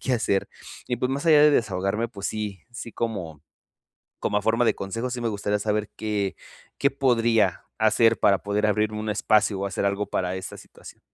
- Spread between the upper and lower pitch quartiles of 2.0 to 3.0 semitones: Yes, average, 2.7 semitones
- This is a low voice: Yes, low, 105 Hz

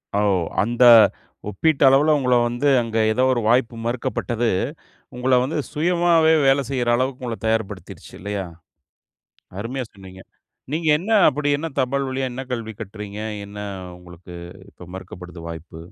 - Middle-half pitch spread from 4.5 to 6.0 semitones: Yes, average, 4.8 semitones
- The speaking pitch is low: Yes, low, 120 Hz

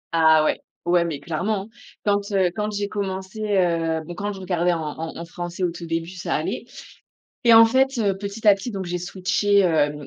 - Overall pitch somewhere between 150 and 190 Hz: Yes, medium, 185 Hz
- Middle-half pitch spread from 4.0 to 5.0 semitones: No, average, 3.3 semitones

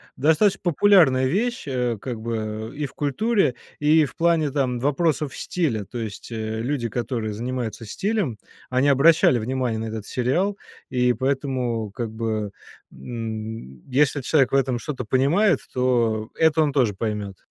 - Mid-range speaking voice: No, low, 130 Hz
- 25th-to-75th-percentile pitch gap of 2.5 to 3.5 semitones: No, average, 4.7 semitones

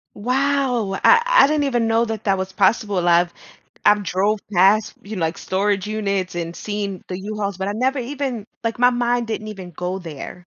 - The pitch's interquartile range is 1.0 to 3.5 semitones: No, average, 4.2 semitones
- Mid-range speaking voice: No, high, 210 Hz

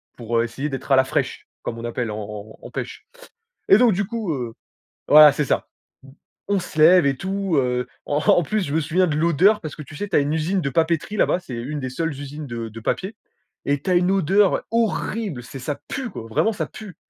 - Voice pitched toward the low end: No, medium, 155 Hz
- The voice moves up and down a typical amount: No, wide, 6.6 semitones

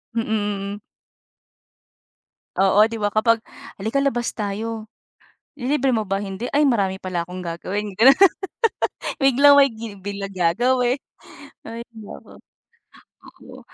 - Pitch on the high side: Yes, high, 220 Hz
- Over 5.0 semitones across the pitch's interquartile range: No, average, 4.0 semitones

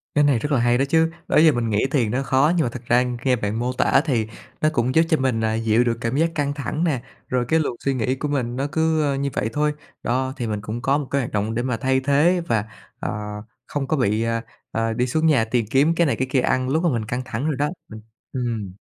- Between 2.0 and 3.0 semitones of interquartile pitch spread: No, average, 3.9 semitones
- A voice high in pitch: No, low, 130 Hz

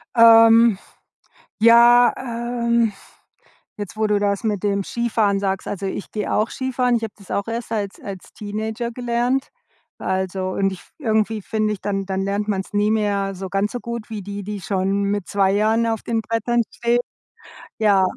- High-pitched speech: Yes, high, 215 Hz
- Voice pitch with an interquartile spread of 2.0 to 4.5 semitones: Yes, average, 2.7 semitones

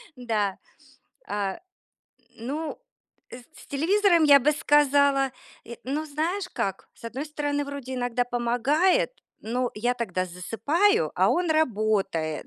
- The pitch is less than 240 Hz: No, very high, 270 Hz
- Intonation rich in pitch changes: No, average, 5.0 semitones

